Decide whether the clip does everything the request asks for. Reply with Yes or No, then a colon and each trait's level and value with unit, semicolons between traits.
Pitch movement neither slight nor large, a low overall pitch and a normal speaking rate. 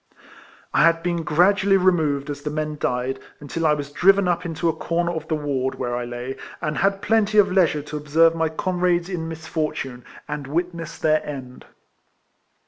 No: average, 3.3 semitones; medium, 160 Hz; average, 180 wpm